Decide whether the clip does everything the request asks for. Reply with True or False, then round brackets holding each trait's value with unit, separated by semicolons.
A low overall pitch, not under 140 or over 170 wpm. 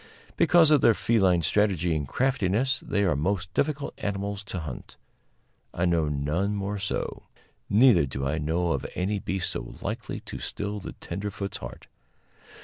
True (95 Hz; 155 wpm)